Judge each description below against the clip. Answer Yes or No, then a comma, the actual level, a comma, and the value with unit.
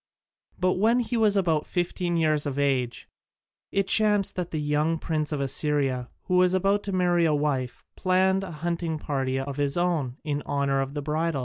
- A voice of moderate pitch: Yes, medium, 160 Hz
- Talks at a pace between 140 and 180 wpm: No, average, 190 wpm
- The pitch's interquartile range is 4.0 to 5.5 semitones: Yes, average, 4.3 semitones